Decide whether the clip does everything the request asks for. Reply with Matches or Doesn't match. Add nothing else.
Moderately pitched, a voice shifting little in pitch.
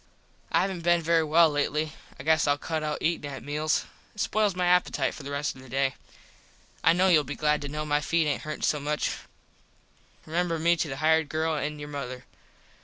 Matches